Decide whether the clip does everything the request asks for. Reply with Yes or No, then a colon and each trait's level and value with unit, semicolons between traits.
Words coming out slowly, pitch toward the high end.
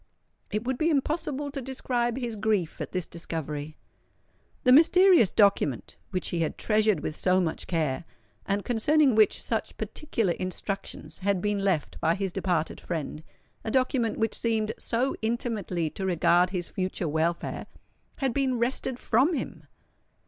No: average, 145 wpm; high, 210 Hz